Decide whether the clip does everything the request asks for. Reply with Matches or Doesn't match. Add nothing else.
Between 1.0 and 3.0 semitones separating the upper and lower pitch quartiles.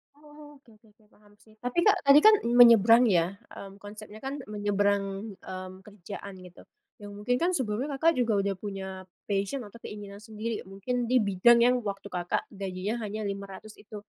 Doesn't match